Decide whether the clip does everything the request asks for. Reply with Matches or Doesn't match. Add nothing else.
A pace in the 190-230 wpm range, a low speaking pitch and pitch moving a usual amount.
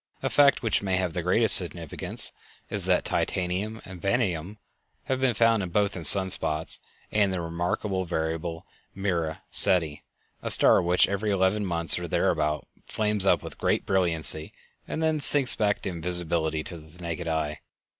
Doesn't match